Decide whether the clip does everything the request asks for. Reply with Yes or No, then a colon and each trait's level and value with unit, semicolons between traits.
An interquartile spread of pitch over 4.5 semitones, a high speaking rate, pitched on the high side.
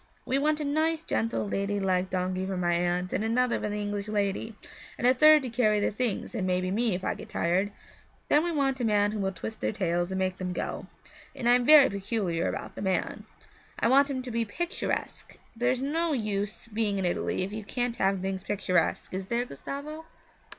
Yes: average, 4.9 semitones; fast, 215 wpm; high, 210 Hz